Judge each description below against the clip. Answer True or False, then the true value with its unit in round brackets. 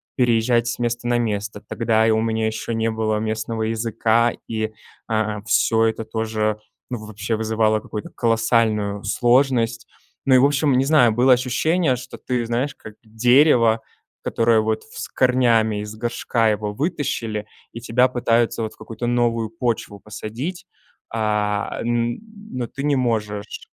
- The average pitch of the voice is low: True (115 Hz)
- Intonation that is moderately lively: False (1.8 semitones)